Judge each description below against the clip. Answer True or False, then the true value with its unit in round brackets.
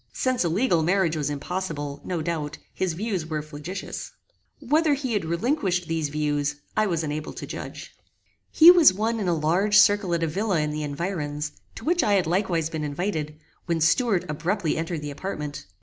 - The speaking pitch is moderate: True (170 Hz)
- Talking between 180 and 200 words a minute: True (185 wpm)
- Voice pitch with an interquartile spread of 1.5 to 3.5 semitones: False (5.0 semitones)